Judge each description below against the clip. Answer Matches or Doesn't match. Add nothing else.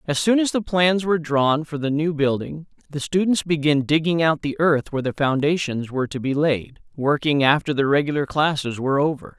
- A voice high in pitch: Doesn't match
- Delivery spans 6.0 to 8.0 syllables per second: Doesn't match